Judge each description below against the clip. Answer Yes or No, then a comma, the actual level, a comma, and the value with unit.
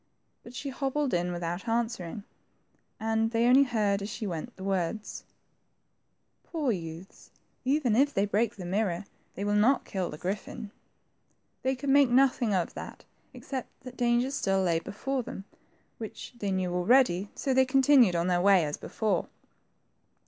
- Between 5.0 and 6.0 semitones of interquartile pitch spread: Yes, wide, 5.4 semitones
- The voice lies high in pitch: Yes, high, 215 Hz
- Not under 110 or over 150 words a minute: No, average, 165 wpm